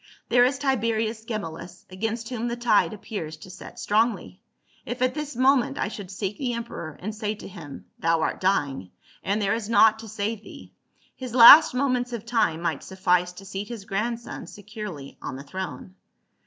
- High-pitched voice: Yes, high, 215 Hz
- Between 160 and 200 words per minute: Yes, average, 185 wpm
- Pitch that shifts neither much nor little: Yes, average, 4.0 semitones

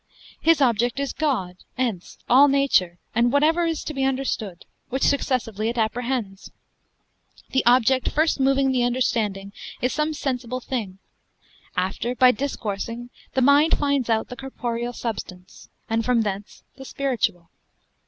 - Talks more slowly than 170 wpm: Yes, average, 140 wpm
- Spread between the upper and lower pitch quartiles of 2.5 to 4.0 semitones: Yes, average, 3.5 semitones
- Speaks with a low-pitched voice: No, very high, 250 Hz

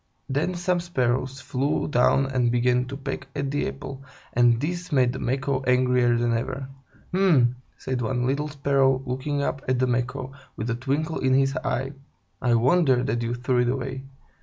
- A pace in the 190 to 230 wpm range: Yes, average, 195 wpm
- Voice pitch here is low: Yes, low, 130 Hz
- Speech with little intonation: Yes, narrow, 2.1 semitones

